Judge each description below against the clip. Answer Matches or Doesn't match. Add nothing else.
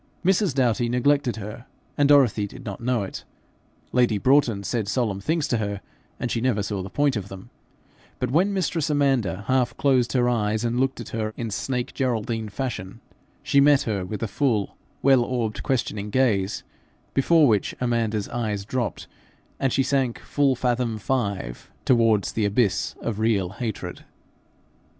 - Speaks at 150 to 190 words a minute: Matches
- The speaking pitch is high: Doesn't match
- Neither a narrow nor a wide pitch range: Matches